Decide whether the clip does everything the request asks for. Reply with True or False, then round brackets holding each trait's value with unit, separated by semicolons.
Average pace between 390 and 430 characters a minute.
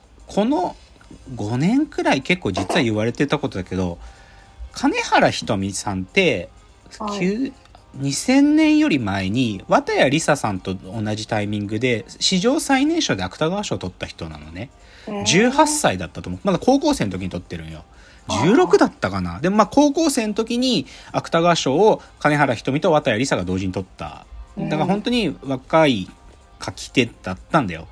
False (300 characters per minute)